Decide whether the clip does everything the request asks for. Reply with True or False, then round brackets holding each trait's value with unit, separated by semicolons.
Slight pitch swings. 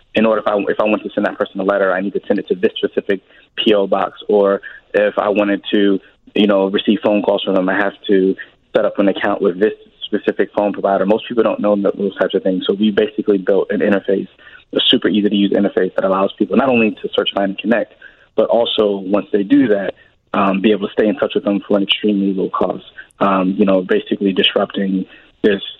True (1.2 semitones)